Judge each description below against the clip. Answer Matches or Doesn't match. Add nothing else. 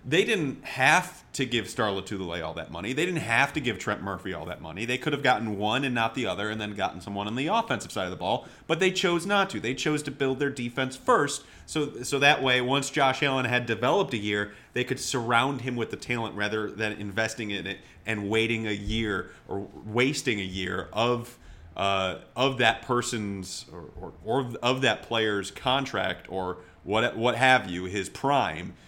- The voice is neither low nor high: Doesn't match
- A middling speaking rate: Doesn't match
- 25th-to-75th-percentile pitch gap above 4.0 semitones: Matches